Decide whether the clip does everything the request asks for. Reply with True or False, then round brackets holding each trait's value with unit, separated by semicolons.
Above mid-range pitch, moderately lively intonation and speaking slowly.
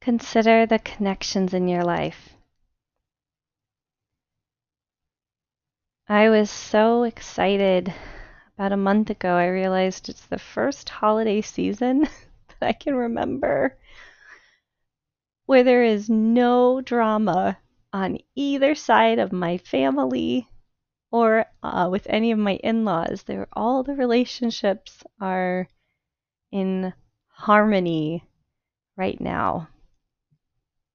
True (210 Hz; 4.1 semitones; 100 wpm)